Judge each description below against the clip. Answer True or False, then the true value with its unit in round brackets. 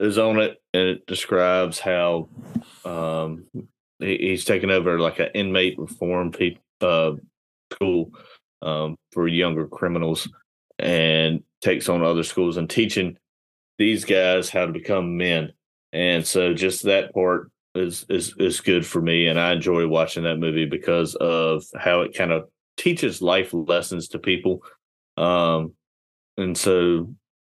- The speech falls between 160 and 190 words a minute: False (145 wpm)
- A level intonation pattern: True (2.1 semitones)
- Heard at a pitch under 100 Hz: True (85 Hz)